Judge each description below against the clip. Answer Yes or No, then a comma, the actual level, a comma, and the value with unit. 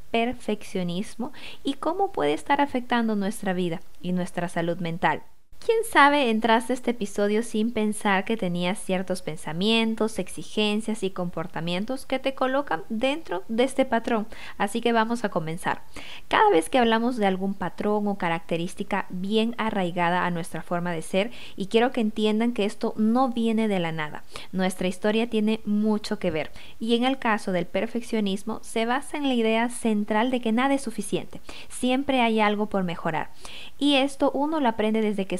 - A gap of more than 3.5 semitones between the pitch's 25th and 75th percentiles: Yes, average, 4.2 semitones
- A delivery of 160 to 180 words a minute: Yes, average, 170 wpm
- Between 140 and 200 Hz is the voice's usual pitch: No, high, 215 Hz